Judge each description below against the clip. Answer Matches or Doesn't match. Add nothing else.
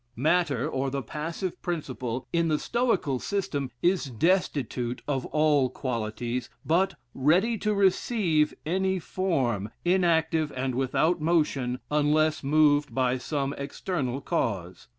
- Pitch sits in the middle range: Matches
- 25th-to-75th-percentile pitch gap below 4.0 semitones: Doesn't match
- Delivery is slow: Matches